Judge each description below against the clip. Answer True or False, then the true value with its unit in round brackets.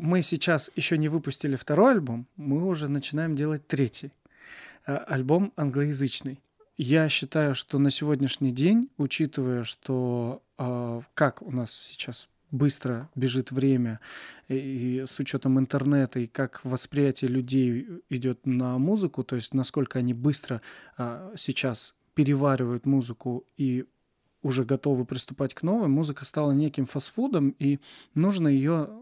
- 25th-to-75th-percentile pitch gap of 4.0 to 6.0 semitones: False (2.7 semitones)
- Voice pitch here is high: False (135 Hz)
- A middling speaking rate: True (130 wpm)